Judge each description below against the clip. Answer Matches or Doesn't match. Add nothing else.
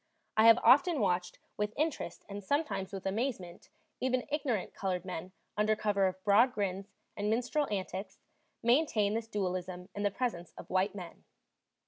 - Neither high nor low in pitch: Doesn't match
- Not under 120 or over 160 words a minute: Matches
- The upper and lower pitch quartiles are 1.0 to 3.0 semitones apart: Doesn't match